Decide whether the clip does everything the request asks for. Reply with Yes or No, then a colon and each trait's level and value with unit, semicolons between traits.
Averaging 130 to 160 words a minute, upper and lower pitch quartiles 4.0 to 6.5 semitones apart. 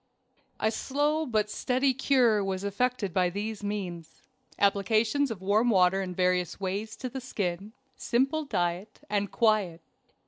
Yes: slow, 135 wpm; average, 4.6 semitones